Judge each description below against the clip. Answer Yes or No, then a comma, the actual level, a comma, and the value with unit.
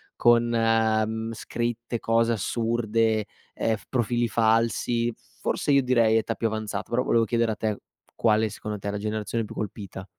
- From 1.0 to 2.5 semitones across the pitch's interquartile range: Yes, narrow, 1.3 semitones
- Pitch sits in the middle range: No, low, 115 Hz